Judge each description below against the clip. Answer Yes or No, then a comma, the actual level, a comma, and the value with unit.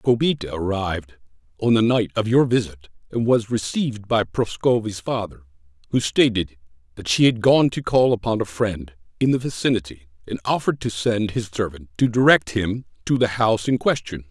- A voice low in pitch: Yes, low, 110 Hz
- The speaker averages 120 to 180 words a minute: Yes, average, 175 wpm